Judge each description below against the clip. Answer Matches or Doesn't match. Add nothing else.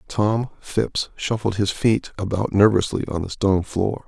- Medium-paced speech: Matches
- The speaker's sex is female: Doesn't match